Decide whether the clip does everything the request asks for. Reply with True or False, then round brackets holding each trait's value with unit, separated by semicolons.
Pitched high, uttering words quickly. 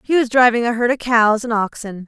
True (235 Hz; 260 wpm)